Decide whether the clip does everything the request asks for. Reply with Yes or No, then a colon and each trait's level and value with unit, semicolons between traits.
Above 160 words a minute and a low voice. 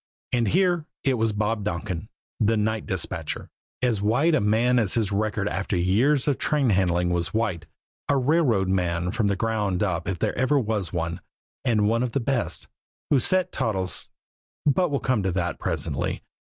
Yes: average, 180 wpm; low, 110 Hz